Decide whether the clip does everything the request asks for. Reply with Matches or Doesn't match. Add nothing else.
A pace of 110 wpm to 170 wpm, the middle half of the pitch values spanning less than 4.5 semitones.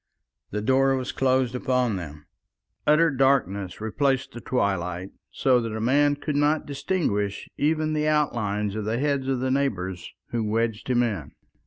Doesn't match